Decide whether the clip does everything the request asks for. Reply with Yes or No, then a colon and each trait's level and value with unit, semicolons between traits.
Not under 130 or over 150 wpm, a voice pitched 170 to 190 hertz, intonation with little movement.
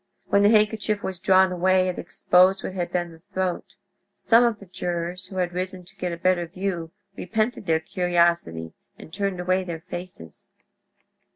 No: average, 175 wpm; medium, 185 Hz; narrow, 1.8 semitones